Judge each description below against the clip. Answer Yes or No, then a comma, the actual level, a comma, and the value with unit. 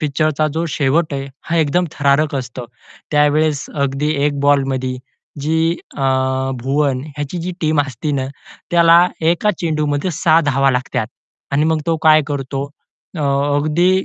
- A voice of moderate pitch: Yes, medium, 150 Hz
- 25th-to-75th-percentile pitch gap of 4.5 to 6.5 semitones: No, narrow, 2.6 semitones